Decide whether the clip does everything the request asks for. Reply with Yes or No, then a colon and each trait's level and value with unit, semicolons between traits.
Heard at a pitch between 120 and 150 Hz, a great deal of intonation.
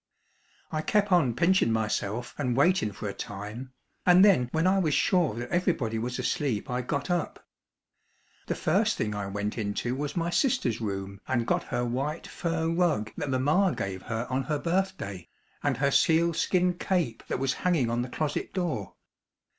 Yes: low, 135 Hz; wide, 7.3 semitones